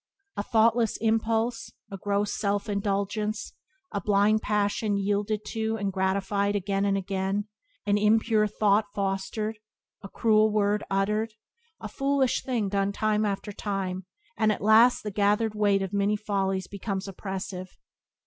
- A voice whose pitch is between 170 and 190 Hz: No, high, 205 Hz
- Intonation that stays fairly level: Yes, narrow, 1.6 semitones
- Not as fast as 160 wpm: Yes, average, 140 wpm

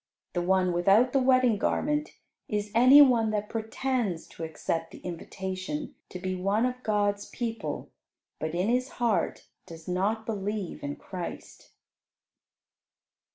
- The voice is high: Yes, high, 205 Hz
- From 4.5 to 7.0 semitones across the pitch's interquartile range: Yes, average, 4.9 semitones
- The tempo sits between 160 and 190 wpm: No, slow, 135 wpm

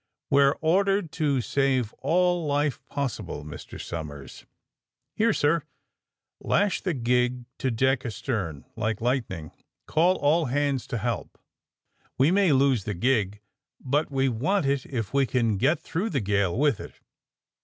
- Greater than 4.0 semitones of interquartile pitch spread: Yes, average, 5.0 semitones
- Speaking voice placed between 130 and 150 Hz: Yes, low, 135 Hz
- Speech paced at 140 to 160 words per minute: Yes, average, 155 wpm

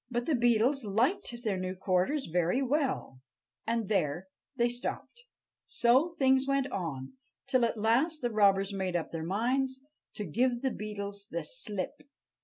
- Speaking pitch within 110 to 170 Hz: No, high, 230 Hz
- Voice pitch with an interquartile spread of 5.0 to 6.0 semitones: Yes, wide, 5.5 semitones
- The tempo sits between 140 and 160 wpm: Yes, average, 155 wpm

